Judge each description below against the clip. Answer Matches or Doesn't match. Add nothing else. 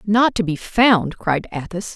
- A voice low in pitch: Doesn't match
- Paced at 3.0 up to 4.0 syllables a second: Matches